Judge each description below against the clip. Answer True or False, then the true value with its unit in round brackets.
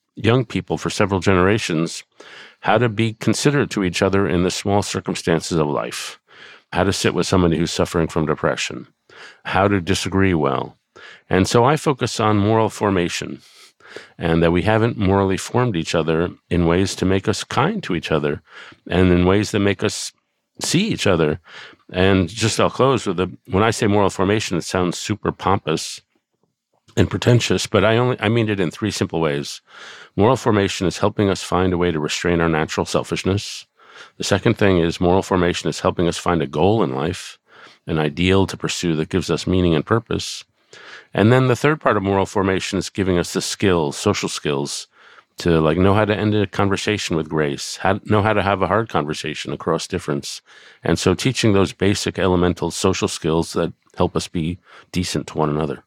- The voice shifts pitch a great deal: False (3.6 semitones)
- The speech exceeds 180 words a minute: True (190 wpm)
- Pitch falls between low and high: False (95 Hz)